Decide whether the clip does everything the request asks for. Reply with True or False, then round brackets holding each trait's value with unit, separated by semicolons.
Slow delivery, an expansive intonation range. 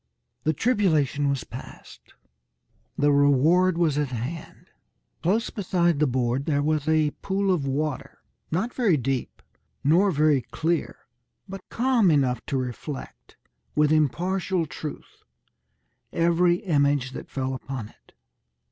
False (125 wpm; 4.3 semitones)